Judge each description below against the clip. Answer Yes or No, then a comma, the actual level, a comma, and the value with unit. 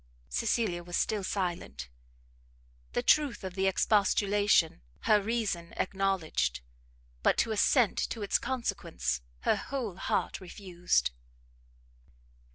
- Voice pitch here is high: Yes, high, 195 Hz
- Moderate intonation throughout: Yes, average, 3.9 semitones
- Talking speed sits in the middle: No, slow, 105 wpm